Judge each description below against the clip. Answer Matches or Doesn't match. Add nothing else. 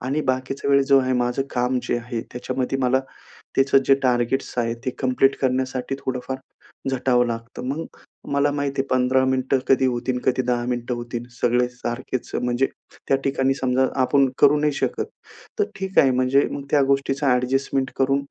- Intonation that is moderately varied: Doesn't match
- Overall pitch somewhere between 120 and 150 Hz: Matches